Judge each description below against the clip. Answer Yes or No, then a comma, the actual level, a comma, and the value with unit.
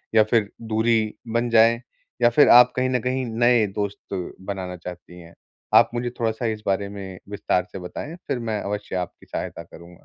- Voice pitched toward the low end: Yes, low, 110 Hz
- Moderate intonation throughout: Yes, average, 3.6 semitones